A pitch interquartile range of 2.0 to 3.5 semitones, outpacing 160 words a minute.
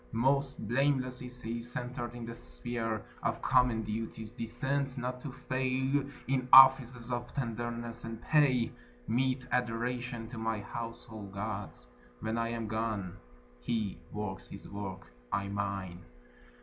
No: narrow, 2.5 semitones; slow, 135 wpm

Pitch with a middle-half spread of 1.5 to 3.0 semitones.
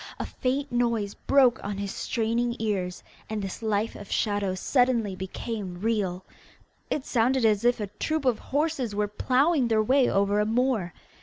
No: average, 3.7 semitones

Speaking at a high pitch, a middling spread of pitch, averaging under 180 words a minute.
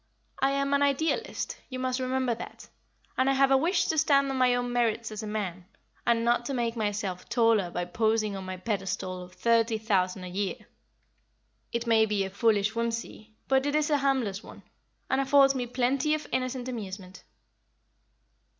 No: high, 235 Hz; average, 4.3 semitones; average, 185 wpm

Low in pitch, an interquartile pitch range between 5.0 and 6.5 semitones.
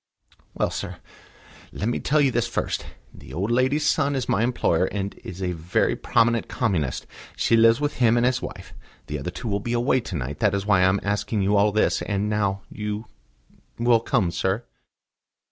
No: low, 105 Hz; average, 3.7 semitones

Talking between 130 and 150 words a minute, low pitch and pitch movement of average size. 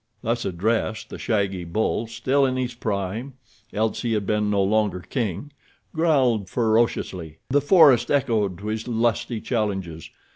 Yes: slow, 135 wpm; low, 110 Hz; average, 3.7 semitones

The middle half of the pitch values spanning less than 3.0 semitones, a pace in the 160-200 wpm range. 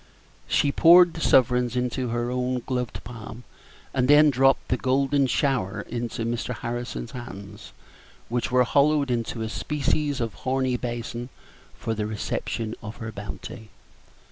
No: narrow, 2.5 semitones; average, 140 wpm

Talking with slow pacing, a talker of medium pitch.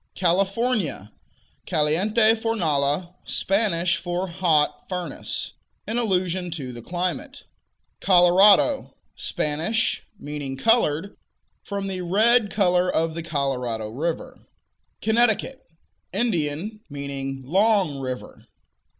Yes: slow, 90 wpm; medium, 180 Hz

